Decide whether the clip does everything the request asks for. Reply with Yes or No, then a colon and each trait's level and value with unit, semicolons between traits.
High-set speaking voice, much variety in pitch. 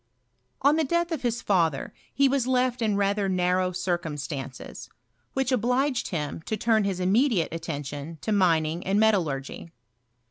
Yes: high, 195 Hz; wide, 6.9 semitones